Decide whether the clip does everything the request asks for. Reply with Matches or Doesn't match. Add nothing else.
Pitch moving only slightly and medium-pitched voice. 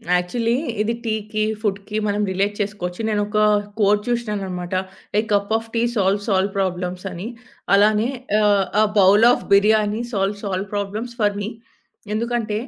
Doesn't match